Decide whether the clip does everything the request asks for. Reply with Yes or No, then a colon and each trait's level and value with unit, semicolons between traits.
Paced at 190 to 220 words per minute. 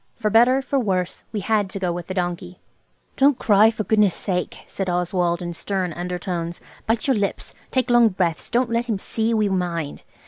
Yes: average, 195 wpm